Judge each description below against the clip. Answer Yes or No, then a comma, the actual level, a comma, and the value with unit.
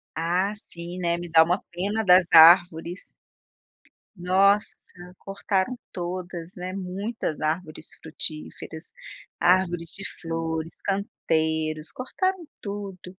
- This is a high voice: No, medium, 180 Hz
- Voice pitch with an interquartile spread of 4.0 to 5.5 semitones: No, average, 2.9 semitones